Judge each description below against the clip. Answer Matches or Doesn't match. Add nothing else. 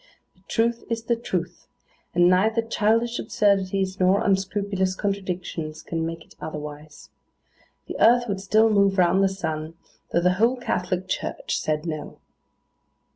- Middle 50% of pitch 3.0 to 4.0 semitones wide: Matches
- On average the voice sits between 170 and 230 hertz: Matches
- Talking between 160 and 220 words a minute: Doesn't match